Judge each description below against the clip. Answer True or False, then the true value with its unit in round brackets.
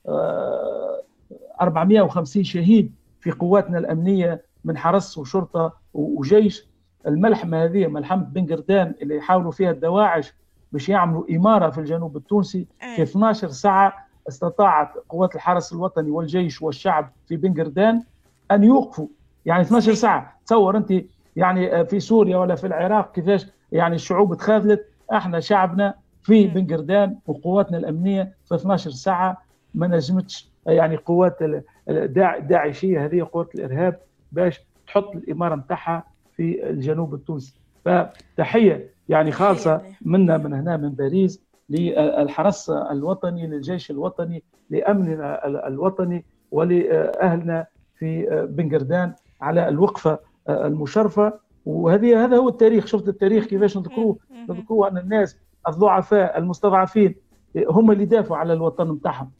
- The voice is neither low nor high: True (180 Hz)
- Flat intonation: False (3.7 semitones)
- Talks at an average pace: True (115 wpm)